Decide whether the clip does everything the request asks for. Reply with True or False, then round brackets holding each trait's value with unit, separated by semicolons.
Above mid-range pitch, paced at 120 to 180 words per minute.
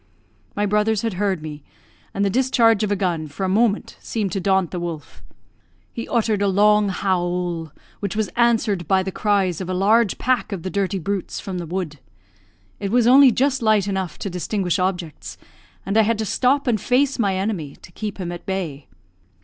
False (195 Hz; 200 wpm)